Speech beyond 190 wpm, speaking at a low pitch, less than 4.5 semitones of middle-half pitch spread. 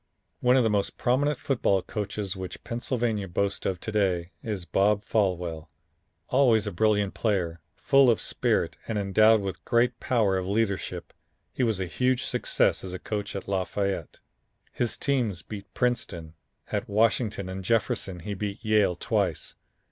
No: average, 160 wpm; low, 105 Hz; average, 3.3 semitones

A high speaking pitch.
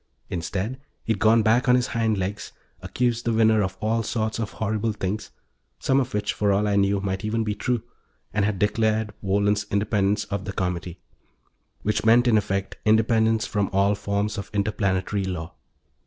No: low, 105 Hz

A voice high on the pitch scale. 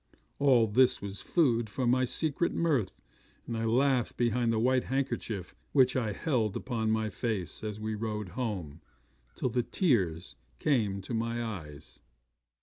No: low, 115 Hz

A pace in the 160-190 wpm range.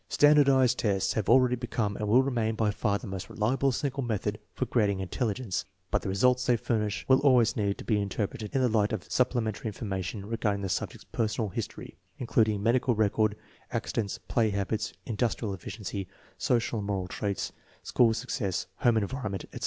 Yes: average, 175 wpm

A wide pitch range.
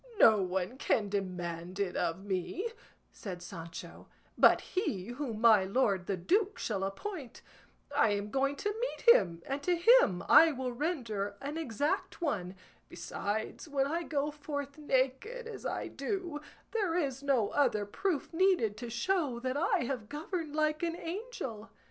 Yes: wide, 8.2 semitones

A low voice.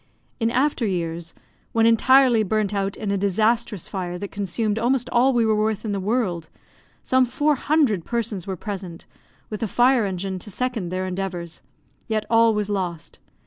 No: high, 210 Hz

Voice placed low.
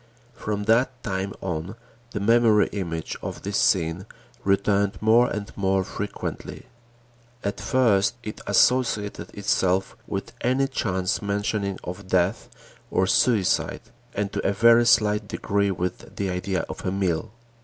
Yes: low, 100 Hz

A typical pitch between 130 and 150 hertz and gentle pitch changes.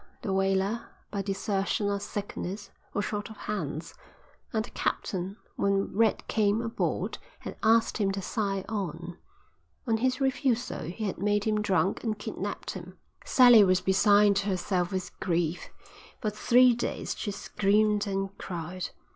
No: high, 200 Hz; narrow, 2.2 semitones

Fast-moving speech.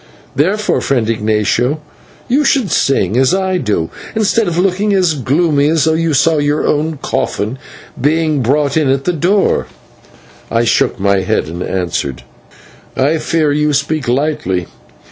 No: average, 150 wpm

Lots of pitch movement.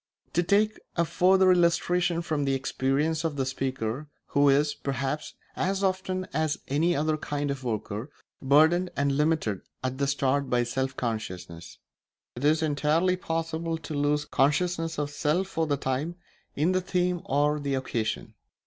No: average, 3.8 semitones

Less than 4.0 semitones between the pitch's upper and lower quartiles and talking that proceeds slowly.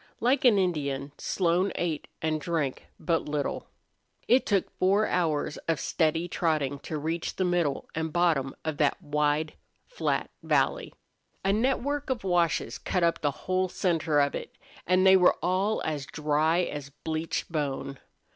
No: average, 3.6 semitones; average, 155 wpm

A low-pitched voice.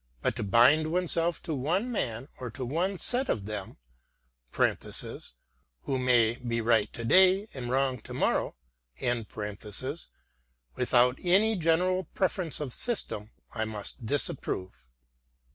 Yes: low, 125 Hz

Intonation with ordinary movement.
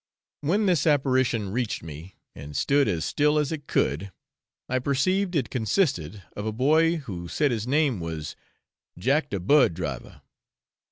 No: wide, 8.2 semitones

